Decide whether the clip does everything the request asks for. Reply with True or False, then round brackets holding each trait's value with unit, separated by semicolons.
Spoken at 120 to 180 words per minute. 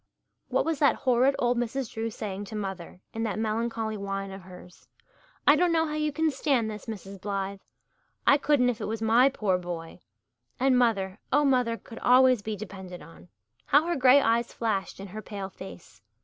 False (190 wpm)